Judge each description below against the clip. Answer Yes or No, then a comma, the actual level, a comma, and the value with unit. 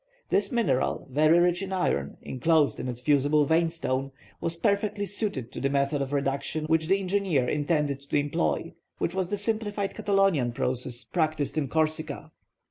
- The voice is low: No, medium, 155 Hz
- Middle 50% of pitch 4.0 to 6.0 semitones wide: Yes, wide, 5.5 semitones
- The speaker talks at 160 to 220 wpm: Yes, average, 165 wpm